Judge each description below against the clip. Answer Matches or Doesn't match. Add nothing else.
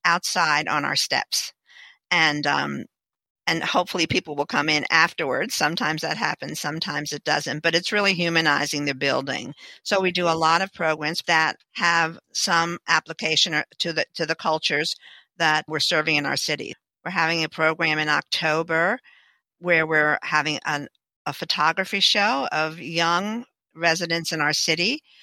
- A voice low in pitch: Doesn't match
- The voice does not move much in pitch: Matches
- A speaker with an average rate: Matches